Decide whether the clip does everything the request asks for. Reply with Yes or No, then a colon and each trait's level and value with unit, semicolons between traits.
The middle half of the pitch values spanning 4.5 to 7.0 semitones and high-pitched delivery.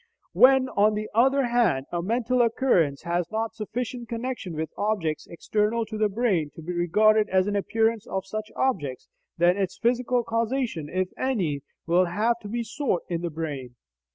Yes: average, 5.2 semitones; high, 210 Hz